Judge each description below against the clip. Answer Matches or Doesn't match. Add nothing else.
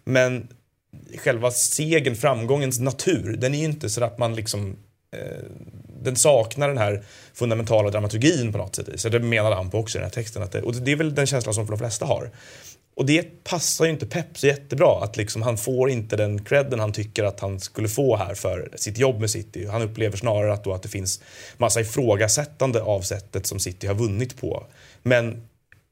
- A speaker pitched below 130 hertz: Matches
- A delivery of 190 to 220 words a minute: Matches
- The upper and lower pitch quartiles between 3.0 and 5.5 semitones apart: Matches